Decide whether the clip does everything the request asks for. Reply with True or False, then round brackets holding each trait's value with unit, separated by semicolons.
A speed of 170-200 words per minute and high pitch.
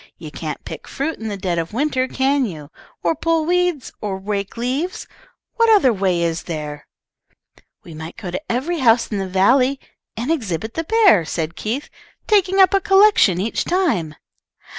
True (175 wpm; 235 Hz)